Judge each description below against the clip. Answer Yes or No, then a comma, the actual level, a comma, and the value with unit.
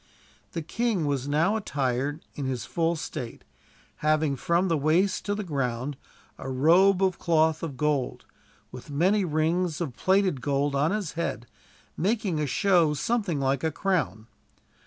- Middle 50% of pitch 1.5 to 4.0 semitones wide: No, average, 4.7 semitones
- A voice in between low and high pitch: Yes, medium, 155 Hz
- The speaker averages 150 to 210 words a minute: Yes, average, 155 wpm